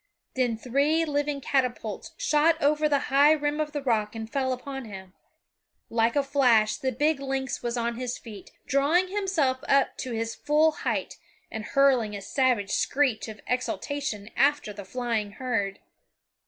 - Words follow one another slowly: No, average, 160 wpm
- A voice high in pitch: Yes, very high, 260 Hz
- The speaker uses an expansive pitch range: No, average, 4.3 semitones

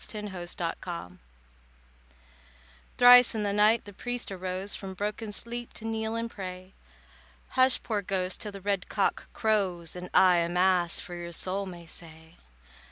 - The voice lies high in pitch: Yes, high, 195 Hz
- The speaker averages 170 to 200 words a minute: No, average, 160 wpm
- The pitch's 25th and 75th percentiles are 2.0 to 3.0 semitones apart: No, average, 3.4 semitones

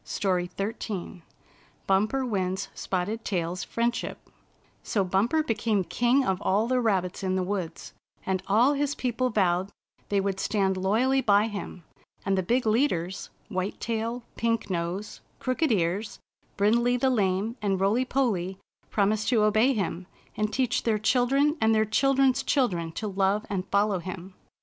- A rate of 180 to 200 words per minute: No, average, 160 wpm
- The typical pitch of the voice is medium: No, high, 210 Hz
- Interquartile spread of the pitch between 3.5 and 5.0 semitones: Yes, average, 4.0 semitones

